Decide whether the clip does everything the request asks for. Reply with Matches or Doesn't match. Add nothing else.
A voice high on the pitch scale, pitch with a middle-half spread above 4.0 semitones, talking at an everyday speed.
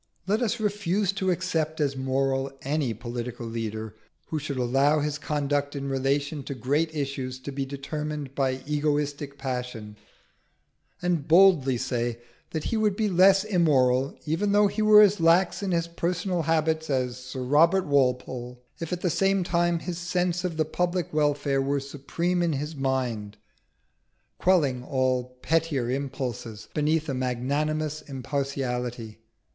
Doesn't match